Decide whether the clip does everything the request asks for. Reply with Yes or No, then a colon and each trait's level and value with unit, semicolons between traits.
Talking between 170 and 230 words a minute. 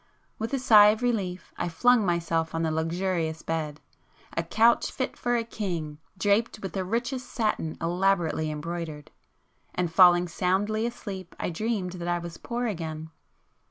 No: average, 150 wpm